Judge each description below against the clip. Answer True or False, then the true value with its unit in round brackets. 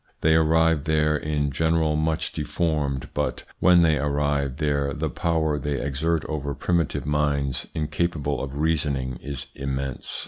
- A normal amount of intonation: False (2.1 semitones)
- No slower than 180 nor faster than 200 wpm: False (140 wpm)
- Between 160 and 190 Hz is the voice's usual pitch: False (75 Hz)